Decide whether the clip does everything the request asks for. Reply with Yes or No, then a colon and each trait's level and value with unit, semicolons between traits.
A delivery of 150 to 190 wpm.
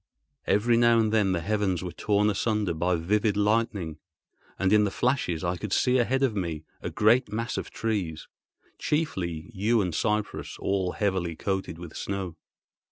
Yes: average, 165 wpm